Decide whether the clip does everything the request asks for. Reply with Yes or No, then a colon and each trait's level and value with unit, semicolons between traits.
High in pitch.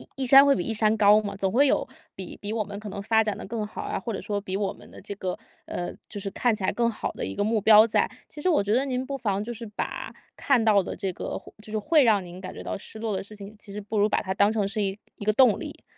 Yes: high, 210 Hz